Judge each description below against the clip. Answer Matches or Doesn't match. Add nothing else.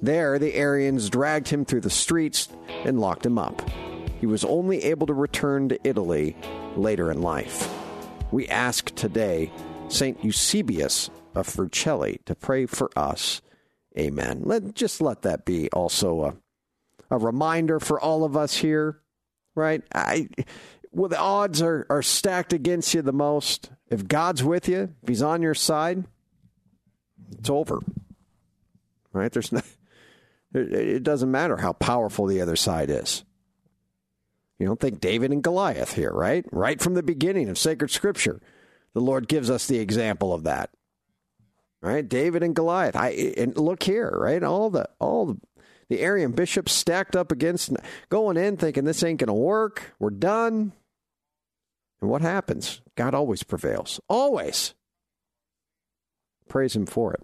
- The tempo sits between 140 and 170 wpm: Matches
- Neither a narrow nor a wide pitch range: Doesn't match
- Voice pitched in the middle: Matches